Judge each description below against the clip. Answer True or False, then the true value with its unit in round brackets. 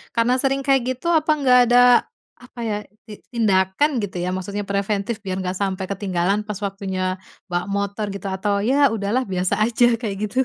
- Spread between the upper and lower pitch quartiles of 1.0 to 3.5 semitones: False (3.9 semitones)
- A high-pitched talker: True (200 Hz)